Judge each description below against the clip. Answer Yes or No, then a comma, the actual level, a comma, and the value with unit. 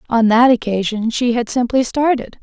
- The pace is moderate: Yes, average, 175 wpm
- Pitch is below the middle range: No, high, 235 Hz